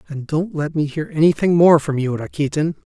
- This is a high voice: No, medium, 155 Hz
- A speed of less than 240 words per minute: Yes, fast, 205 wpm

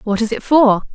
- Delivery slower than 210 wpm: No, fast, 255 wpm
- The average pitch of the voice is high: Yes, high, 230 Hz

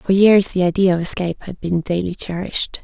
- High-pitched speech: No, medium, 180 Hz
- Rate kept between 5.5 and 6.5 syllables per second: Yes, 5.9 syllables/s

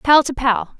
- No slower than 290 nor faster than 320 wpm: No, fast, 225 wpm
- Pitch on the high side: Yes, very high, 255 Hz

